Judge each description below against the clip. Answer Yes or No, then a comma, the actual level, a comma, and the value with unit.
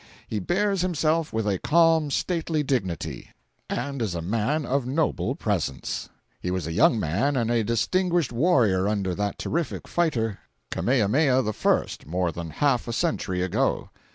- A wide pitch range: Yes, wide, 7.9 semitones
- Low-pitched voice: Yes, low, 120 Hz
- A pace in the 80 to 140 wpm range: No, average, 155 wpm